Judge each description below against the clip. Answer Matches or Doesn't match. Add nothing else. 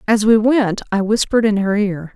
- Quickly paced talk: Matches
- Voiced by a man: Doesn't match